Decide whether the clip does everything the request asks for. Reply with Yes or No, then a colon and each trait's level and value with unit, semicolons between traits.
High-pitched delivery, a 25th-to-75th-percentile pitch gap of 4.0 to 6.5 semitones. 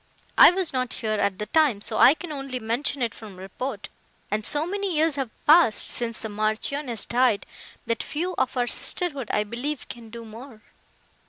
Yes: high, 245 Hz; average, 5.2 semitones